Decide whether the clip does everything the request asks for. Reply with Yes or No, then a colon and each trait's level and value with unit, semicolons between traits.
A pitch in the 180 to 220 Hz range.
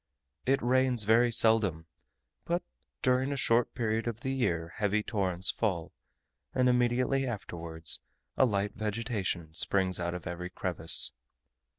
No: low, 110 Hz